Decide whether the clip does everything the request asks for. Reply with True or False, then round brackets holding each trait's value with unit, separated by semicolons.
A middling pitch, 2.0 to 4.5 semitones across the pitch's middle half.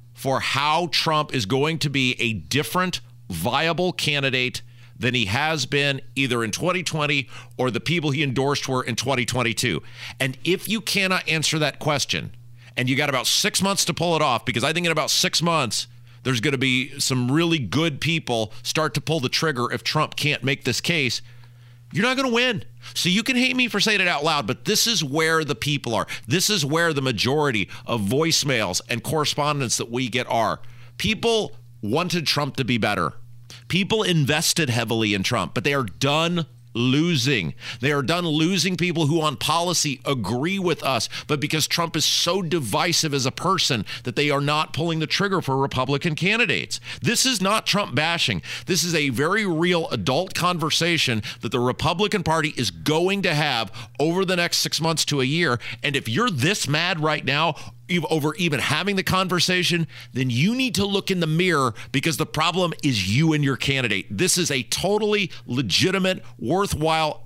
False (145 Hz; 5.3 semitones)